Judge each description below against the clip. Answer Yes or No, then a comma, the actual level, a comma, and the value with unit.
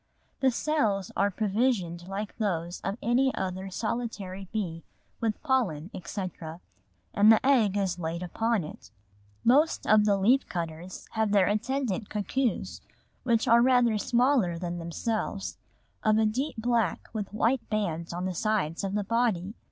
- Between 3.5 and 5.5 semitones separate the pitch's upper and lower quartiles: Yes, average, 4.2 semitones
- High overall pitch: Yes, high, 210 Hz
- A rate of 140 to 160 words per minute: Yes, average, 150 wpm